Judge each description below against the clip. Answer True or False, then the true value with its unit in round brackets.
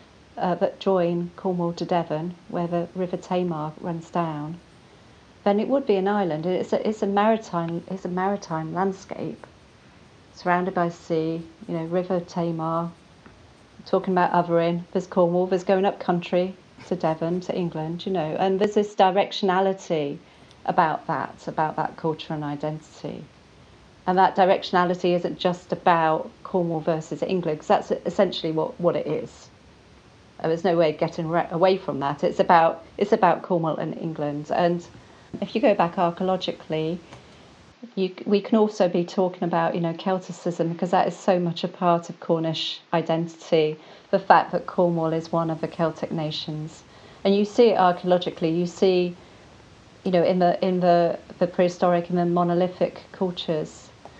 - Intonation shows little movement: True (2.3 semitones)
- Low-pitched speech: False (175 Hz)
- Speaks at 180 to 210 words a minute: False (160 wpm)